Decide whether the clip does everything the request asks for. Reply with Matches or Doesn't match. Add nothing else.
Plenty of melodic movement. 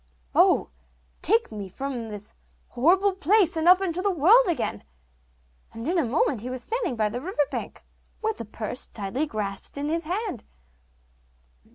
Matches